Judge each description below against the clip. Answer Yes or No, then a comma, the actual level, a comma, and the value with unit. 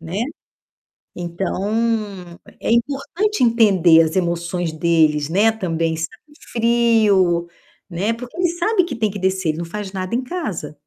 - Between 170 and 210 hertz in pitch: Yes, high, 190 Hz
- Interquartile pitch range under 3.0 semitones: No, wide, 5.5 semitones